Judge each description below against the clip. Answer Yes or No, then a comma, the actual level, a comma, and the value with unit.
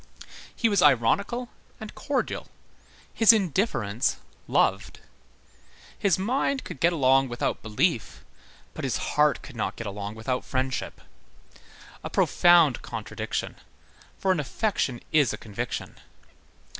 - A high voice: No, medium, 150 Hz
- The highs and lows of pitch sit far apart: Yes, wide, 8.7 semitones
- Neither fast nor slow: No, slow, 120 wpm